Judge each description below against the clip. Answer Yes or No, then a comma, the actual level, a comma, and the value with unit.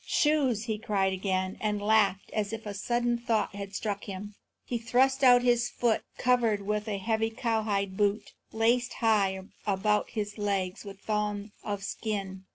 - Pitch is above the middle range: Yes, high, 210 Hz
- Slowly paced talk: No, average, 165 wpm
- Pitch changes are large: No, narrow, 2.5 semitones